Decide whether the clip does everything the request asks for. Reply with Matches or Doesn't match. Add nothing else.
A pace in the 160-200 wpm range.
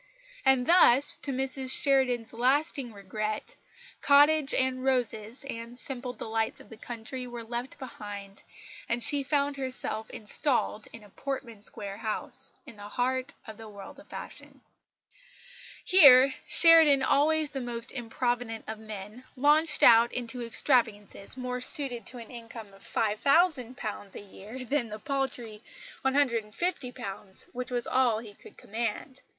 Doesn't match